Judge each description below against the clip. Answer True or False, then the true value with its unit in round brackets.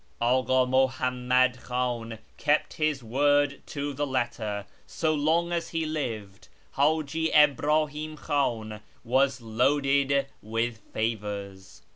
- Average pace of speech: False (105 wpm)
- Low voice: True (130 Hz)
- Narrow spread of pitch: False (3.9 semitones)